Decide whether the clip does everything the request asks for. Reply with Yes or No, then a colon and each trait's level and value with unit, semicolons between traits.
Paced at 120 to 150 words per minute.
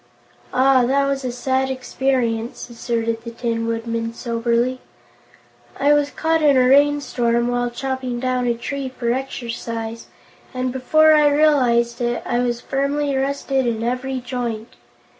Yes: average, 140 wpm